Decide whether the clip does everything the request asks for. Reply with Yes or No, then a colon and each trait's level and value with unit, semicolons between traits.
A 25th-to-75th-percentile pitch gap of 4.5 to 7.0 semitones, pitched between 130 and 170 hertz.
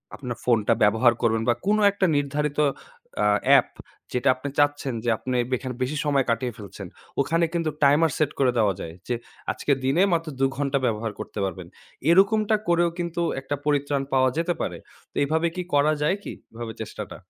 Yes: average, 4.8 semitones; medium, 140 Hz